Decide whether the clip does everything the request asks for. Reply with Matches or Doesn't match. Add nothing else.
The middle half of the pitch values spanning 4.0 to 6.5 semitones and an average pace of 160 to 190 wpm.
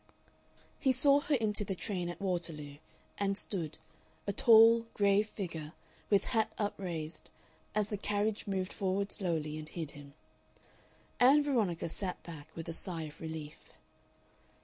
Doesn't match